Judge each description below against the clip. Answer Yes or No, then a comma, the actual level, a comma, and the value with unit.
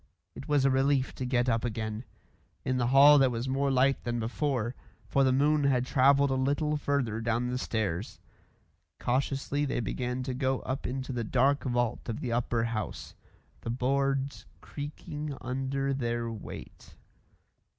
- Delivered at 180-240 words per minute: No, average, 160 wpm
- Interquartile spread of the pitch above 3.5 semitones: No, narrow, 2.5 semitones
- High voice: No, low, 130 Hz